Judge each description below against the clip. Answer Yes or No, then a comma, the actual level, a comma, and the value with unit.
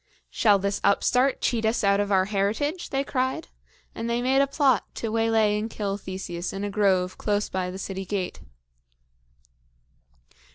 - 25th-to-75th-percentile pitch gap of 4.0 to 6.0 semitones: No, average, 3.5 semitones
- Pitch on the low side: No, high, 210 Hz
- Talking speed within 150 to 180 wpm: Yes, average, 165 wpm